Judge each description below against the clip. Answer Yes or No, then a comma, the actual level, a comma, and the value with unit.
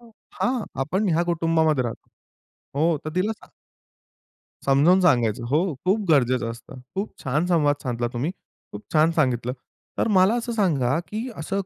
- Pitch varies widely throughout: Yes, wide, 6.6 semitones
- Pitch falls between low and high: Yes, medium, 160 Hz